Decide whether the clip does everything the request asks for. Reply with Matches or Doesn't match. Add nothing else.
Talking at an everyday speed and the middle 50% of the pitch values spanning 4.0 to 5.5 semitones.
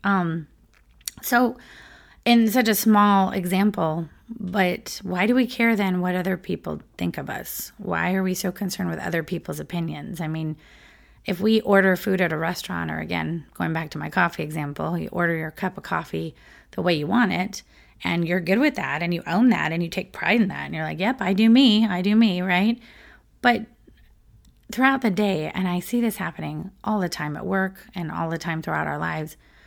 Doesn't match